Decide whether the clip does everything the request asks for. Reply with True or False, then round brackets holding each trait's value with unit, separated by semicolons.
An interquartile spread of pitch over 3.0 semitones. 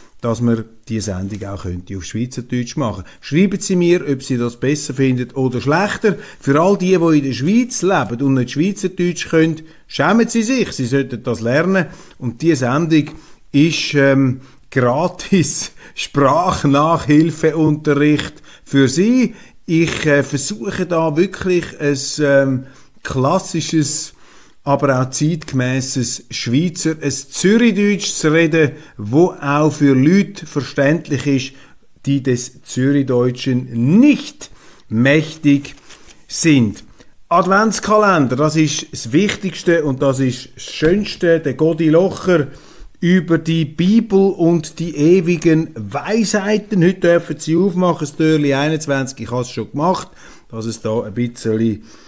True (4.7 semitones)